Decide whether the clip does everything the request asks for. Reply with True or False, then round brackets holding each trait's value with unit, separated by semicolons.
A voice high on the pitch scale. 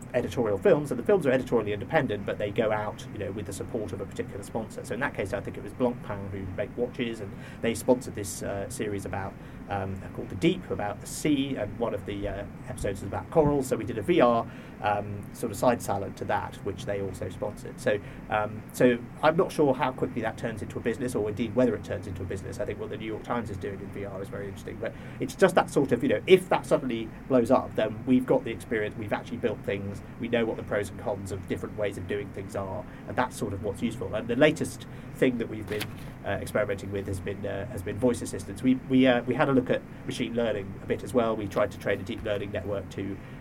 False (110 Hz)